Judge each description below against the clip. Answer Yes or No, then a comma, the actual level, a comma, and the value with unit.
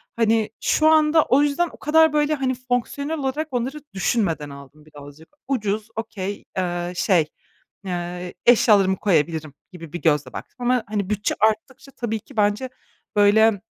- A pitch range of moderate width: No, wide, 6.8 semitones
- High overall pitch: Yes, high, 215 Hz